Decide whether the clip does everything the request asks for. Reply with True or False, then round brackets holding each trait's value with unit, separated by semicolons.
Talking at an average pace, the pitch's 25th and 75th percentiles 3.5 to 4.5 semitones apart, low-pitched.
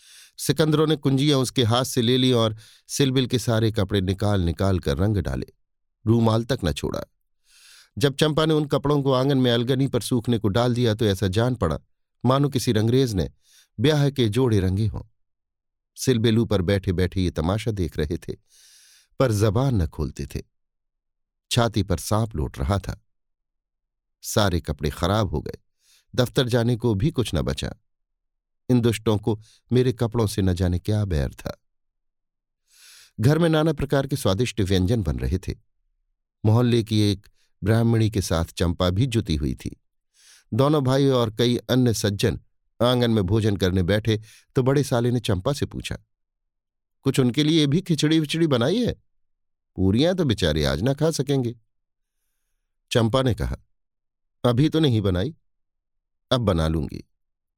False (160 wpm; 5.3 semitones; 110 Hz)